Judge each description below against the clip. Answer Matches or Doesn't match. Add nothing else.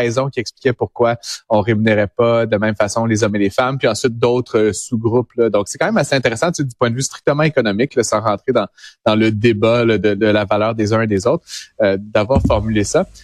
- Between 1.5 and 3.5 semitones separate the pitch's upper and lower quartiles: Matches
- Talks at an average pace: Doesn't match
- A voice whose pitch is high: Doesn't match